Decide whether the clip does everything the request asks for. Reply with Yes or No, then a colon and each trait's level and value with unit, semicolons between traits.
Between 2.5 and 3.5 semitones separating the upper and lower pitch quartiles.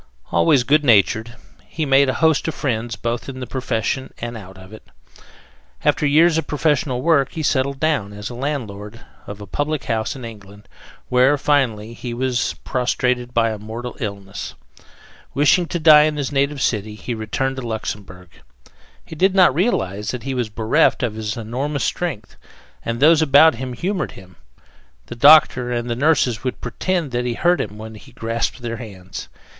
No: average, 4.7 semitones